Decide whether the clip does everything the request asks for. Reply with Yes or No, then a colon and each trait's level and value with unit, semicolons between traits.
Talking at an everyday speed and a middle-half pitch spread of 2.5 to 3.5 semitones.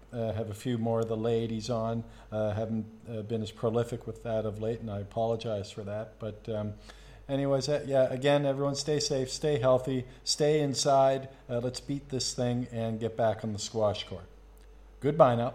Yes: average, 195 wpm; average, 3.2 semitones